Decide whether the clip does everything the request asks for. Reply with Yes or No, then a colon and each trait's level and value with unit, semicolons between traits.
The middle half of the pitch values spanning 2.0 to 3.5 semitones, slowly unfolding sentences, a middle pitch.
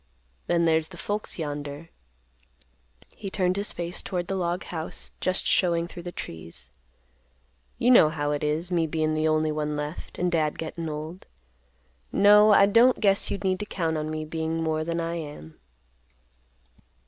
No: average, 2.9 semitones; average, 170 wpm; medium, 165 Hz